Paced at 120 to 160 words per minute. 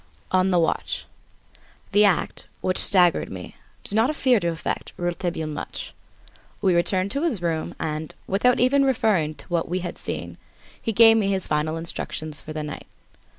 No: average, 170 wpm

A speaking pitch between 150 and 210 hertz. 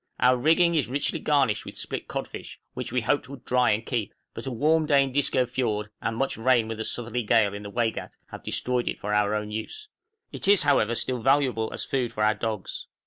No: low, 120 Hz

